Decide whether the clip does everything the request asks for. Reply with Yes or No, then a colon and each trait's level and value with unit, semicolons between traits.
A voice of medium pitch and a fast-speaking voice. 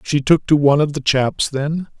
Yes: medium, 145 Hz; fast, 240 wpm